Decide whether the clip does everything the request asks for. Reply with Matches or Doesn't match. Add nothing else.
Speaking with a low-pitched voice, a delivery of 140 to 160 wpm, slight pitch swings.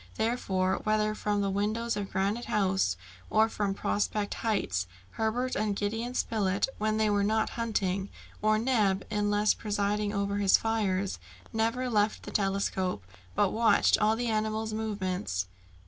Doesn't match